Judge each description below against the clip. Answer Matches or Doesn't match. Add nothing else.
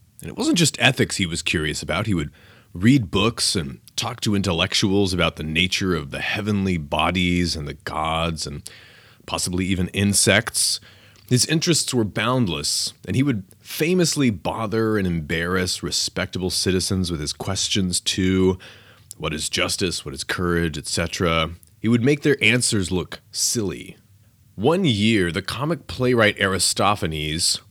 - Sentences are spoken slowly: Doesn't match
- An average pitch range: Matches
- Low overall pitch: Matches